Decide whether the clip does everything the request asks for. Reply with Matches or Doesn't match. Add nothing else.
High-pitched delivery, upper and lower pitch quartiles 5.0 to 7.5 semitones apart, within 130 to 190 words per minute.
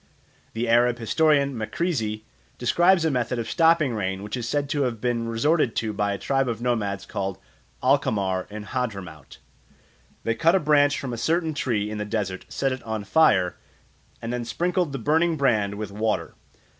Doesn't match